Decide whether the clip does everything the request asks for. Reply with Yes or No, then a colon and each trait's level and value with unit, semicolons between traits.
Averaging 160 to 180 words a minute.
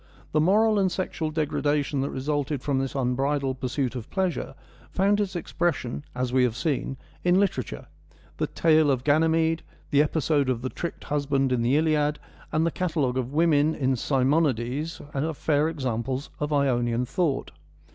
Yes: average, 165 wpm